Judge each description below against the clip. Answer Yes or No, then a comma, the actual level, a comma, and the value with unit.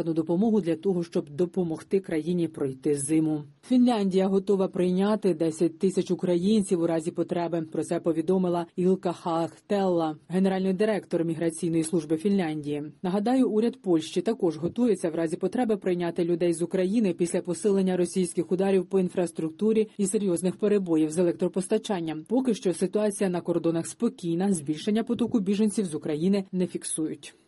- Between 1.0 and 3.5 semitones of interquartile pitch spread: Yes, average, 2.8 semitones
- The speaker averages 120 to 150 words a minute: Yes, average, 140 wpm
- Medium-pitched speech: Yes, medium, 180 Hz